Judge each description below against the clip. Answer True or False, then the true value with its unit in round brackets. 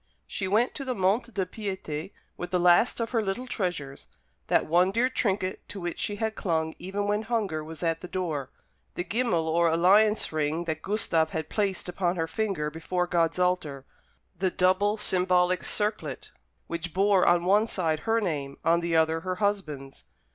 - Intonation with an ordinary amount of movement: True (3.9 semitones)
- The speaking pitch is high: False (180 Hz)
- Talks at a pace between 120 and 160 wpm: False (180 wpm)